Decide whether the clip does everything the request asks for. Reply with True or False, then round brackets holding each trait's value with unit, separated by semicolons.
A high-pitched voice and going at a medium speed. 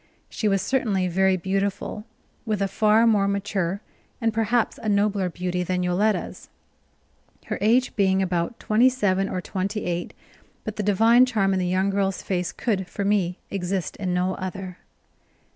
True (195 Hz; 160 wpm)